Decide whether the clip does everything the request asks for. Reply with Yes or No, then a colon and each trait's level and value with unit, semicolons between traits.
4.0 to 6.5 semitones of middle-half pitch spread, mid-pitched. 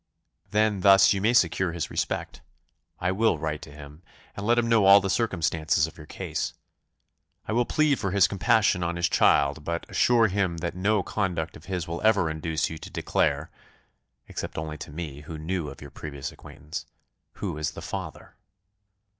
No: average, 4.3 semitones; very low, 85 Hz